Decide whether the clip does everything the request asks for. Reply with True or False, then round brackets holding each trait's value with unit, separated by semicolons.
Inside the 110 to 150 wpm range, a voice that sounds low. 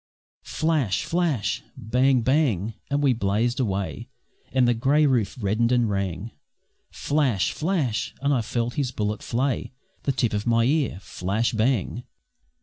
True (145 wpm; 120 Hz)